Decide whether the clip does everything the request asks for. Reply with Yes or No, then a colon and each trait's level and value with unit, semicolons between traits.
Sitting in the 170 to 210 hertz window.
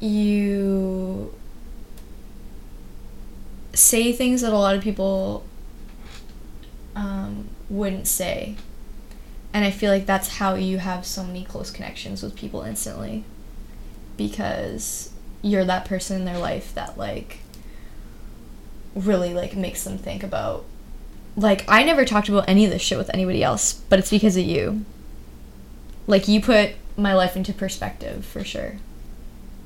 Yes: high, 190 Hz